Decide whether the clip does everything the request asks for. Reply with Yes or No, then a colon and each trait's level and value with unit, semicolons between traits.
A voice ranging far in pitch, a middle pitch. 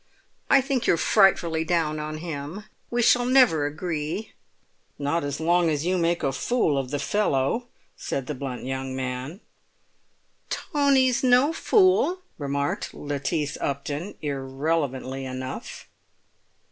Yes: wide, 7.2 semitones; medium, 155 Hz